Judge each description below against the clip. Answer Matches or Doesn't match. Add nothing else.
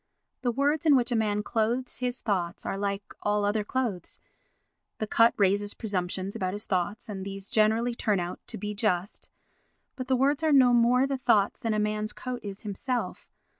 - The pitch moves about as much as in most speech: Matches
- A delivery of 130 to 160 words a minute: Doesn't match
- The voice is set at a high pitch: Matches